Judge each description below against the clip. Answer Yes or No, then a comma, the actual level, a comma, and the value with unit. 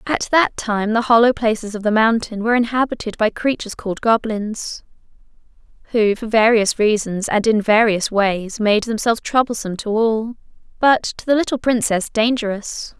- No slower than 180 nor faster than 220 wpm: No, average, 155 wpm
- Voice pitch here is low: No, high, 220 Hz